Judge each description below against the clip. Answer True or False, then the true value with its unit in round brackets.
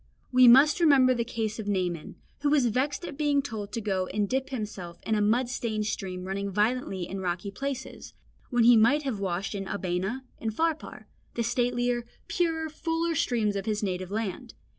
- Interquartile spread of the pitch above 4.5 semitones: True (5.0 semitones)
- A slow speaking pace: False (185 wpm)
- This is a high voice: True (225 Hz)